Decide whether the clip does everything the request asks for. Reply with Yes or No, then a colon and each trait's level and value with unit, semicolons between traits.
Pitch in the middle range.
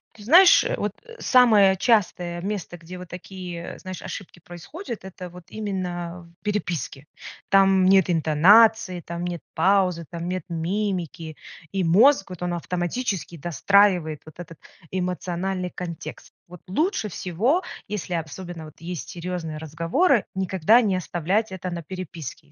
Yes: medium, 180 Hz